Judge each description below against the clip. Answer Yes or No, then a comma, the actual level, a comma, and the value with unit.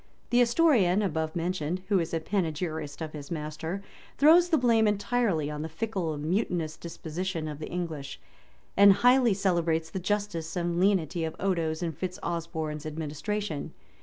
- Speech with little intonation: No, average, 4.1 semitones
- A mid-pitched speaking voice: Yes, medium, 170 Hz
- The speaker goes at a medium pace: Yes, average, 160 wpm